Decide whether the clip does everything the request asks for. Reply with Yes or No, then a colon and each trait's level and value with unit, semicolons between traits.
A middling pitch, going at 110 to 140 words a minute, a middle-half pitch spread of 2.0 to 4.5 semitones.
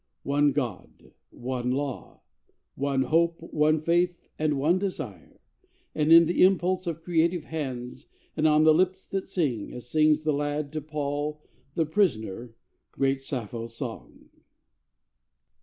Yes: medium, 150 Hz; slow, 135 wpm; average, 3.8 semitones